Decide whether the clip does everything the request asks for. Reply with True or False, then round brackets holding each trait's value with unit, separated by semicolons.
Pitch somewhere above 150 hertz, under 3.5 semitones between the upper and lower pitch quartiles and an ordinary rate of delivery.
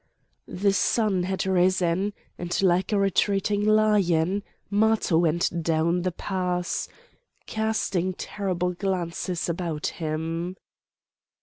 False (185 Hz; 2.6 semitones; 100 wpm)